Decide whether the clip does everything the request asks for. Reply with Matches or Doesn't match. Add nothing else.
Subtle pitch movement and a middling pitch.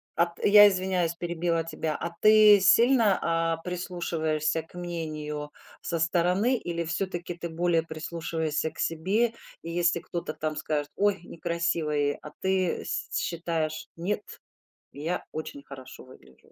Matches